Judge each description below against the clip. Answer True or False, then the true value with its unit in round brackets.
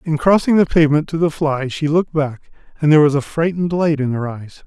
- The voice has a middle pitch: True (155 Hz)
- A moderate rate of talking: False (245 wpm)